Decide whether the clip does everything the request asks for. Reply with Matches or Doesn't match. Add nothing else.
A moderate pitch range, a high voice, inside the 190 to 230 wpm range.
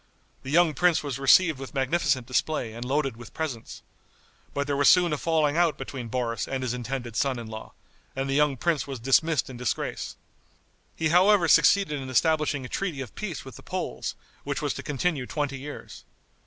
Doesn't match